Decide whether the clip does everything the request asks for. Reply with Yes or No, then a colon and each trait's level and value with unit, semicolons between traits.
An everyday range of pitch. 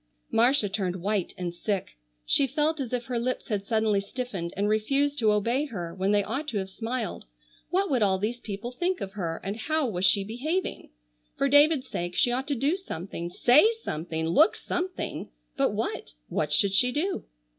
No: wide, 6.2 semitones